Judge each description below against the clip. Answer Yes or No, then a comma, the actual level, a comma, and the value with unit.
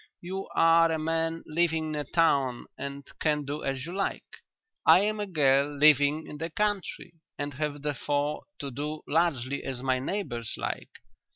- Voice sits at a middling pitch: Yes, medium, 150 Hz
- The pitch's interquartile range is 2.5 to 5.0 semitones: Yes, average, 2.8 semitones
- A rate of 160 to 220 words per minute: Yes, average, 170 wpm